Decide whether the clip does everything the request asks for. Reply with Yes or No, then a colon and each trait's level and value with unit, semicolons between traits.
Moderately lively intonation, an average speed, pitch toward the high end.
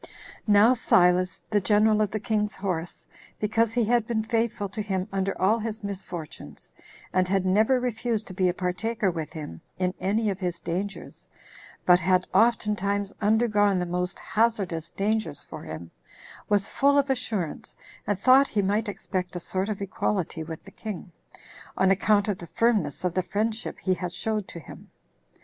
Yes: average, 3.2 semitones; average, 175 wpm; high, 200 Hz